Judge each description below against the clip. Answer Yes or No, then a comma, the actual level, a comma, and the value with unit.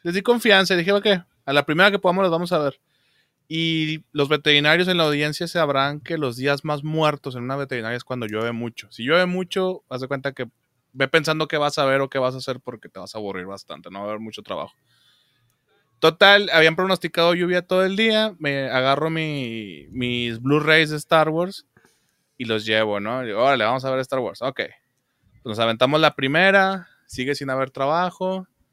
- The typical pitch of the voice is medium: Yes, medium, 145 Hz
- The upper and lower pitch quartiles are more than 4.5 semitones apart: Yes, average, 5.2 semitones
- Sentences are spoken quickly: Yes, fast, 210 wpm